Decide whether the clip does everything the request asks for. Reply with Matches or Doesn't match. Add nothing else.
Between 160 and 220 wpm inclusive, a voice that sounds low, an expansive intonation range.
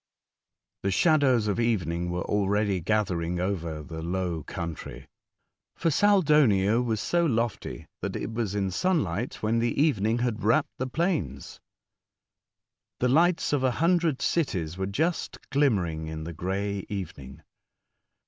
Doesn't match